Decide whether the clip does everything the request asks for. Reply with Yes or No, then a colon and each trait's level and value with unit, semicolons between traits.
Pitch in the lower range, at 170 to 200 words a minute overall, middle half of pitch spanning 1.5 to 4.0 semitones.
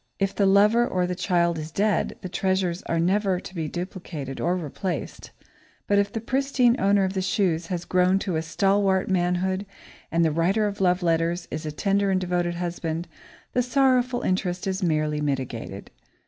No: medium, 185 Hz; average, 180 wpm; average, 2.8 semitones